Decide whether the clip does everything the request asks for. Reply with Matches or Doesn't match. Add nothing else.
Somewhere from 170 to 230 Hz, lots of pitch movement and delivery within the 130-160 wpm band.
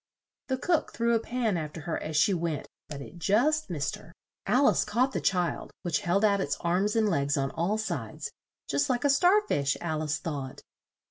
Doesn't match